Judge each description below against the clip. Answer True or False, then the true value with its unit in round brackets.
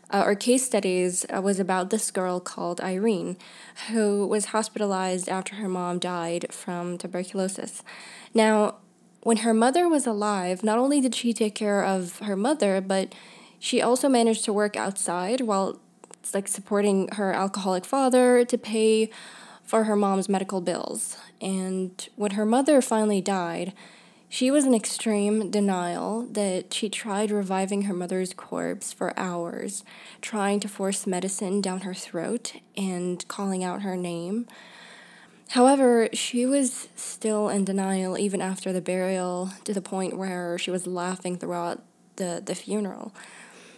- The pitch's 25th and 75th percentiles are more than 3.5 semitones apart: False (3.2 semitones)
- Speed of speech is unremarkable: True (150 wpm)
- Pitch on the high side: True (200 Hz)